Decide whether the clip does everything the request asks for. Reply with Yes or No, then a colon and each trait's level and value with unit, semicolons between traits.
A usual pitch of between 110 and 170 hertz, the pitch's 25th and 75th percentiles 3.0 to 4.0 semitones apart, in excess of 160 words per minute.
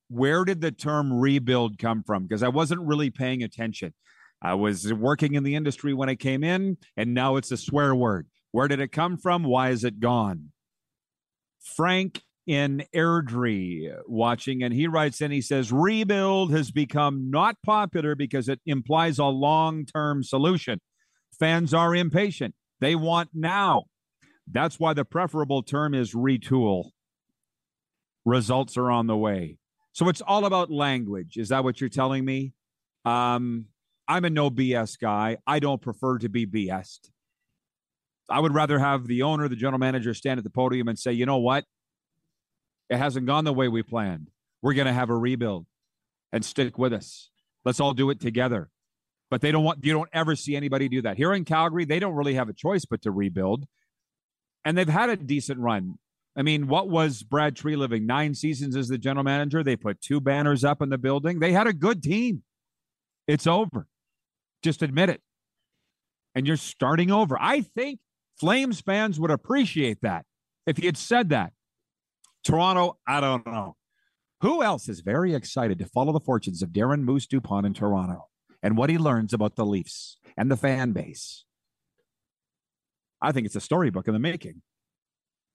No: medium, 140 Hz; average, 4.7 semitones; average, 180 wpm